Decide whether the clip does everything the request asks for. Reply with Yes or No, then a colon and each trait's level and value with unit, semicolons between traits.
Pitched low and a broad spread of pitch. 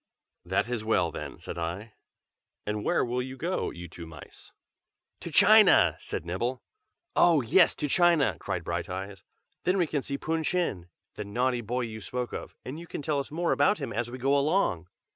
Yes: low, 125 Hz; wide, 6.8 semitones